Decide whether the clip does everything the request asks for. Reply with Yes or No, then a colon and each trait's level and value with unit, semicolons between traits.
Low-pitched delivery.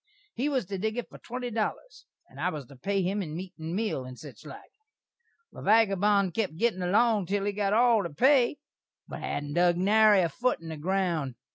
No: high, 195 Hz